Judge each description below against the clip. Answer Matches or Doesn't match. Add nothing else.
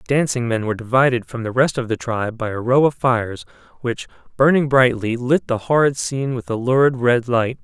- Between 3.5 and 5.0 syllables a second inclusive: Doesn't match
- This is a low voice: Matches